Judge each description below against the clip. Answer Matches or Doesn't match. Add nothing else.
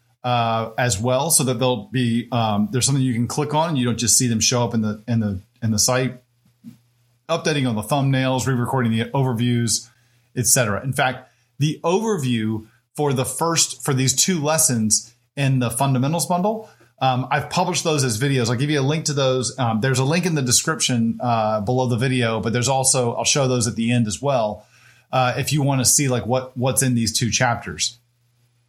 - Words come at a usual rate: Doesn't match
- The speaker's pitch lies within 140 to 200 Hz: Doesn't match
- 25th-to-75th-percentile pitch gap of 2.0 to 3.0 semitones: Matches